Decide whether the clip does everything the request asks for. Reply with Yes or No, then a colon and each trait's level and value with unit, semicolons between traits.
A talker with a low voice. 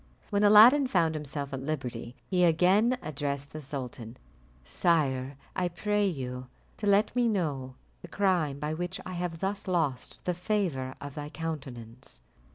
No: medium, 155 Hz